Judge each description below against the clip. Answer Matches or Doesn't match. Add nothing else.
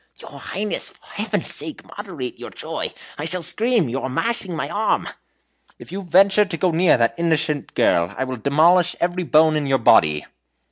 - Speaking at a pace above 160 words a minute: Matches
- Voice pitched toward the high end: Doesn't match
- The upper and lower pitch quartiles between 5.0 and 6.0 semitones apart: Matches